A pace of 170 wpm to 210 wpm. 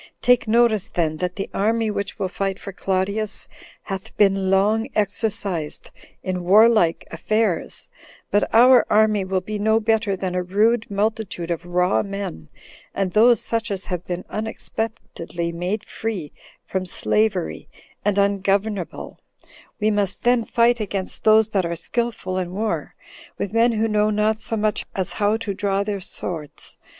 No: average, 155 wpm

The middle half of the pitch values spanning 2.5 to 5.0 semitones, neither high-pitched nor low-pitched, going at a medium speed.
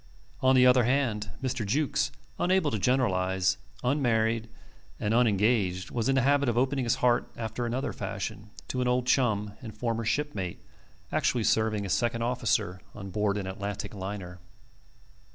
No: average, 3.7 semitones; low, 115 Hz; average, 155 wpm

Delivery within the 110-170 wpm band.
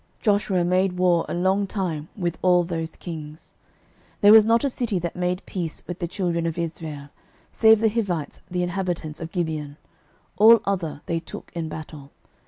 No: average, 185 wpm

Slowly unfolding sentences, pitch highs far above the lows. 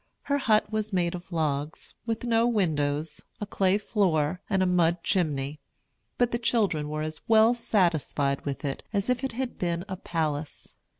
No: average, 175 wpm; wide, 6.0 semitones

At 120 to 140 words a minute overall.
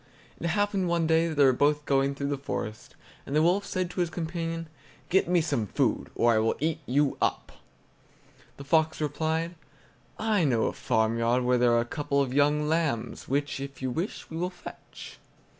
No: average, 195 wpm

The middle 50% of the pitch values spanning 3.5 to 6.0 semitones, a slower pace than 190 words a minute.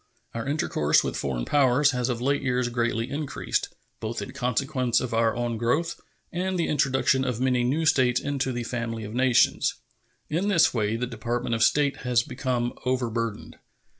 No: average, 2.7 semitones; average, 170 wpm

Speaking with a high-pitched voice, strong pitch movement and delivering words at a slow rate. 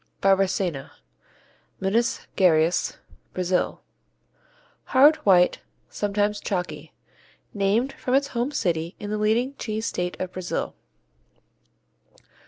No: high, 195 Hz; average, 3.8 semitones; slow, 95 wpm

